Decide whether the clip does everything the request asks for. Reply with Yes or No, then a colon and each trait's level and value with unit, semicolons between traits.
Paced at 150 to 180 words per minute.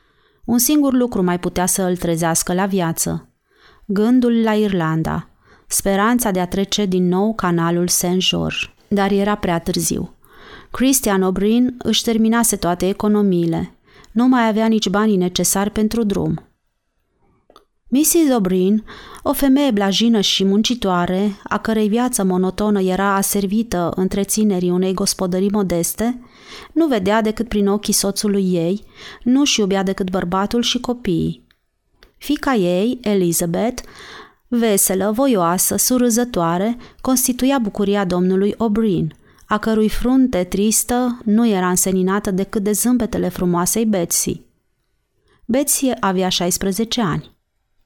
No: average, 120 wpm